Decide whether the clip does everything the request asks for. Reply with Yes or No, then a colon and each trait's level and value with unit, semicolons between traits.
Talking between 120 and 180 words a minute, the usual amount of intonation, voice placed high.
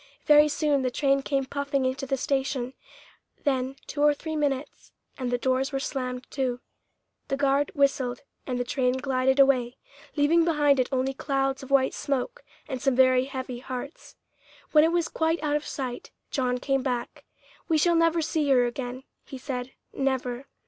No: average, 175 wpm; narrow, 2.1 semitones; very high, 270 Hz